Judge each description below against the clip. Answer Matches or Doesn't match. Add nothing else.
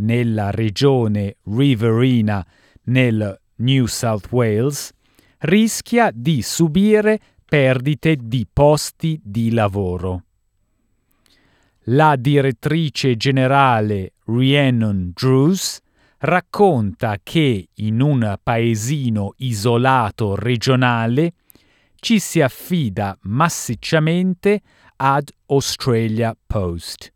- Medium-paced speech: Doesn't match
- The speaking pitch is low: Matches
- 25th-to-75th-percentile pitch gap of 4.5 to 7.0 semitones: Matches